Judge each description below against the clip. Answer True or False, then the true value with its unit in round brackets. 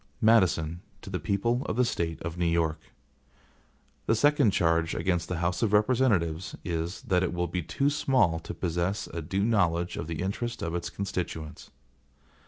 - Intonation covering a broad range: False (4.0 semitones)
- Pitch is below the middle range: True (90 Hz)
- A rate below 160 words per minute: False (175 wpm)